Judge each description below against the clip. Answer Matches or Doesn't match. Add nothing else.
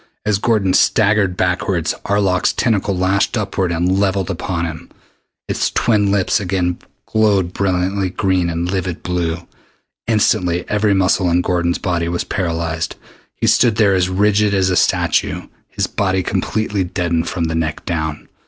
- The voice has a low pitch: Matches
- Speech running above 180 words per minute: Doesn't match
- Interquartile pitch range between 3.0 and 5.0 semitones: Doesn't match